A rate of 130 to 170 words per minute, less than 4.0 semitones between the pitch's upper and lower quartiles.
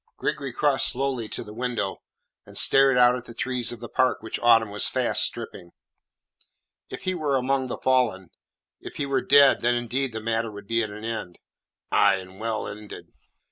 No: average, 190 wpm; average, 3.4 semitones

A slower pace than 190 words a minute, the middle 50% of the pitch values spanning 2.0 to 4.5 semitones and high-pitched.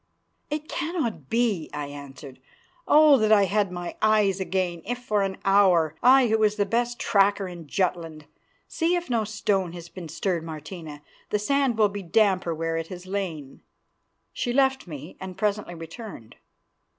No: average, 165 wpm; average, 4.9 semitones; high, 195 Hz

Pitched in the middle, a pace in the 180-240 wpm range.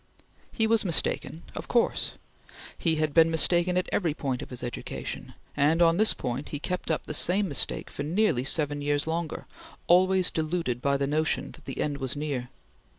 Yes: medium, 155 Hz; average, 185 wpm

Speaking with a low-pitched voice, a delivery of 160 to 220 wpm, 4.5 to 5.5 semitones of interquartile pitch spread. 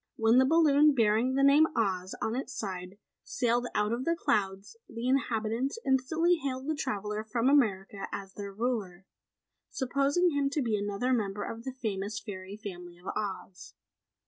No: high, 230 Hz; average, 165 wpm; average, 5.1 semitones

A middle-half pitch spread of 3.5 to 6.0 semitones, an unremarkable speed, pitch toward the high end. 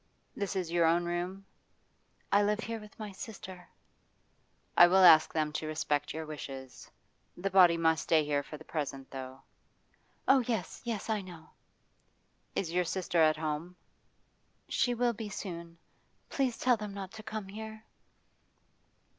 No: average, 4.9 semitones; average, 155 wpm; medium, 180 Hz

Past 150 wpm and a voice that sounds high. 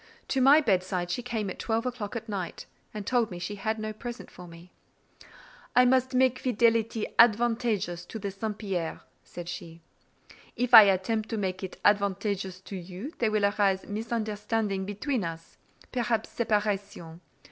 Yes: average, 160 wpm; high, 210 Hz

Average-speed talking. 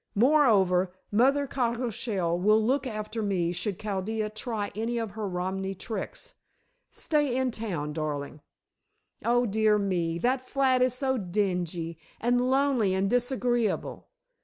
No: slow, 130 wpm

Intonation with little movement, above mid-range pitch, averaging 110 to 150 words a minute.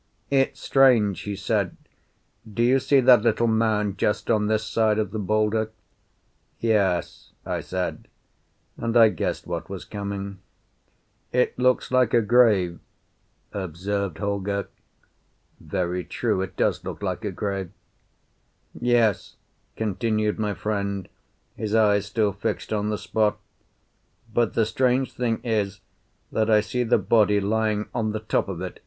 No: narrow, 2.2 semitones; low, 105 Hz; average, 140 wpm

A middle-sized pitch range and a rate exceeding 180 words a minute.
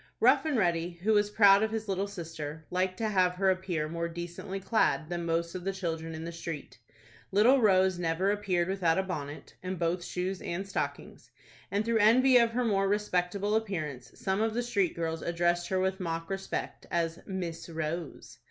Yes: average, 3.2 semitones; average, 190 wpm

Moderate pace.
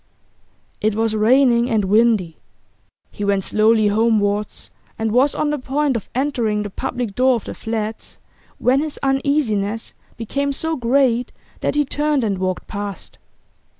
Yes: average, 150 wpm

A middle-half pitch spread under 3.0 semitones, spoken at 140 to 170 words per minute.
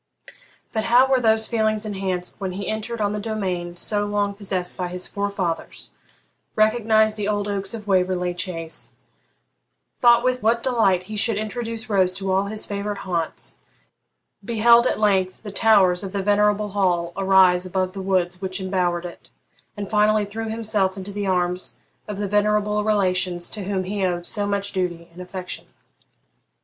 Yes: narrow, 2.6 semitones; average, 165 wpm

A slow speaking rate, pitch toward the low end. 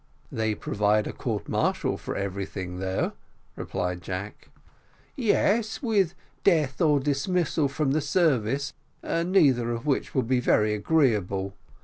Yes: slow, 125 wpm; low, 130 Hz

